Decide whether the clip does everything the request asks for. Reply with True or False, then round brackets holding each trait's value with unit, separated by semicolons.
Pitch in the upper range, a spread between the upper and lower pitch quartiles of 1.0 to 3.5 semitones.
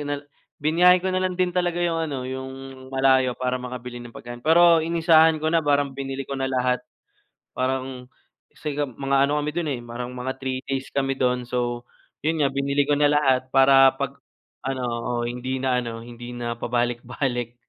False (135 Hz; 2.8 semitones)